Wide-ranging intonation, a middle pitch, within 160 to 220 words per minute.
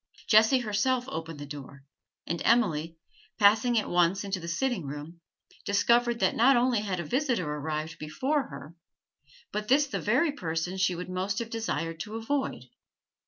No: wide, 6.5 semitones; high, 200 Hz; average, 165 wpm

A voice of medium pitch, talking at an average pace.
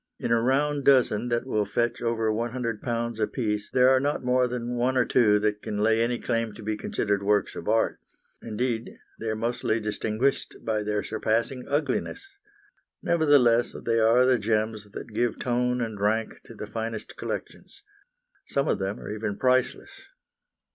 No: low, 115 Hz; average, 170 wpm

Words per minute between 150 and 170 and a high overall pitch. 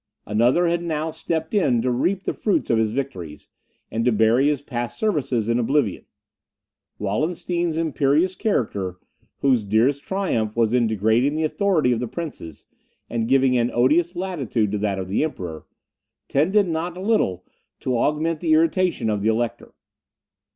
No: average, 160 wpm; low, 135 Hz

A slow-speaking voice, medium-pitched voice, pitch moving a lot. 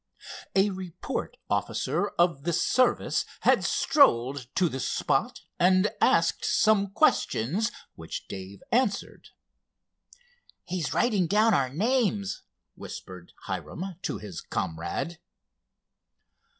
Yes: slow, 100 wpm; medium, 180 Hz; wide, 8.1 semitones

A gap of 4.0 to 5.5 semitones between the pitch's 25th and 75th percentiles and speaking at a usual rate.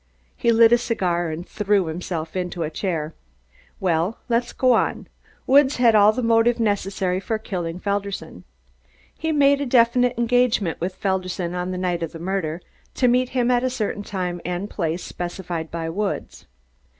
Yes: average, 5.1 semitones; average, 170 wpm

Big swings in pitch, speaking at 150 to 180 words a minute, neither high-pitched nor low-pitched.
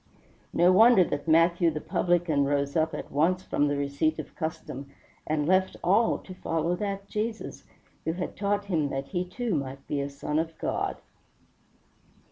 No: average, 4.2 semitones; average, 170 wpm; medium, 165 Hz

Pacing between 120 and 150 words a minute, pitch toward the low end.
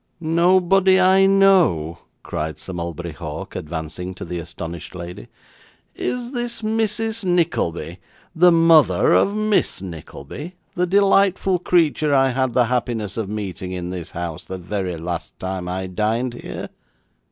Yes: average, 140 wpm; low, 120 Hz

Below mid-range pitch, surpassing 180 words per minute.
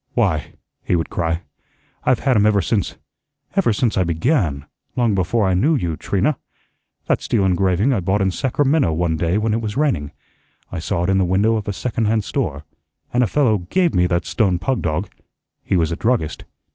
Yes: low, 100 Hz; average, 200 wpm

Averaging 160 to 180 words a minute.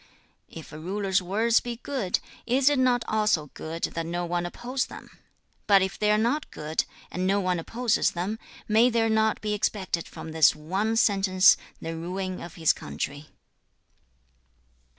Yes: average, 170 wpm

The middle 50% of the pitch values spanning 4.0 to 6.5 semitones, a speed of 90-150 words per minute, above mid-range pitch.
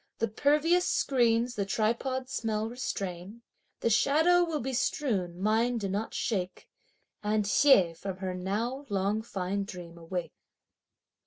Yes: average, 5.1 semitones; slow, 135 wpm; high, 220 Hz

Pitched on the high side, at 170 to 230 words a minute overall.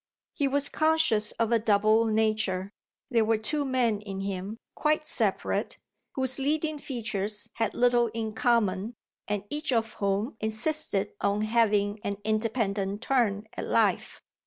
No: high, 220 Hz; average, 140 wpm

